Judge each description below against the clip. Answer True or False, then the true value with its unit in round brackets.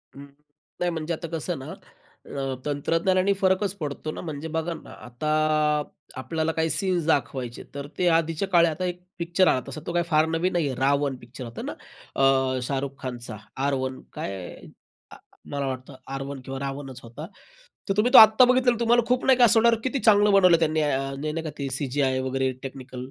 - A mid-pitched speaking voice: True (155 Hz)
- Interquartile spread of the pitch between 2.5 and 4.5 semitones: False (5.1 semitones)